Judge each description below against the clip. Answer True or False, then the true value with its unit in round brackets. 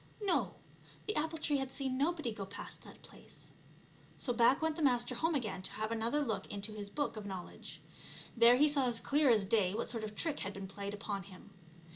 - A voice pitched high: True (235 Hz)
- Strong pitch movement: True (5.9 semitones)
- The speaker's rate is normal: False (215 wpm)